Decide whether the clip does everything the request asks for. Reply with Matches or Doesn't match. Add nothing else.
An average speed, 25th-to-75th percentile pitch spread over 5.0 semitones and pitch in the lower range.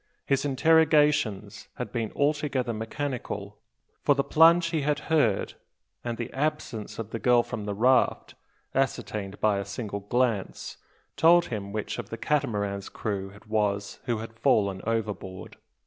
Matches